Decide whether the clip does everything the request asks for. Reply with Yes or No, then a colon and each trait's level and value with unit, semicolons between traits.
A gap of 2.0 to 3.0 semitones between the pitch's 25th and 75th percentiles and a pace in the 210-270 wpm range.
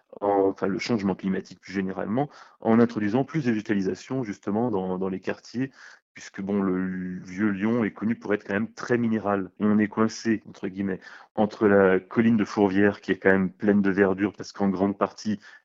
No: narrow, 2.6 semitones; average, 195 wpm